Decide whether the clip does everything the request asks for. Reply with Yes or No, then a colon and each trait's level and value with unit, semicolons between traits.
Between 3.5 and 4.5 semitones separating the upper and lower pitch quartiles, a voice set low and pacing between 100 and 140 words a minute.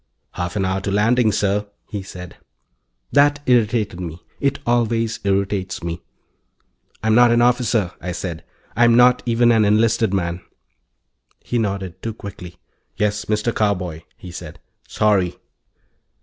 Yes: average, 4.0 semitones; low, 105 Hz; slow, 135 wpm